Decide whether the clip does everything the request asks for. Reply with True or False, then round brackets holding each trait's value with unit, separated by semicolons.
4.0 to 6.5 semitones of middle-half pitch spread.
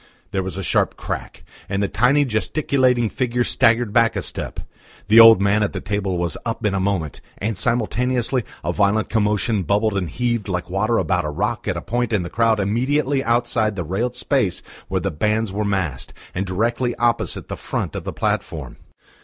False (3.5 semitones)